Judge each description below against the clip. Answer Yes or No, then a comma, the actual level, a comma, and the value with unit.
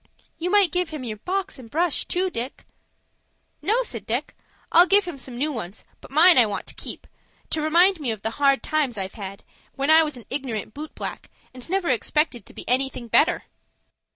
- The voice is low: No, very high, 285 Hz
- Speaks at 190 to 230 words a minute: Yes, fast, 205 wpm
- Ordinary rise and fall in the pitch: No, wide, 6.3 semitones